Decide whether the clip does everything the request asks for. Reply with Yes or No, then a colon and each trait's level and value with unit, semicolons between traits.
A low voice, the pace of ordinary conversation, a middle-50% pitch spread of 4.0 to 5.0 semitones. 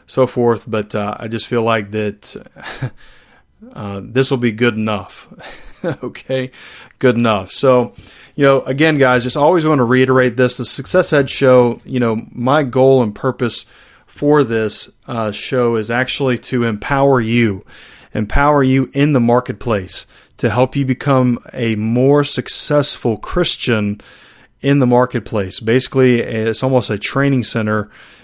No: low, 125 Hz; average, 150 wpm; average, 2.9 semitones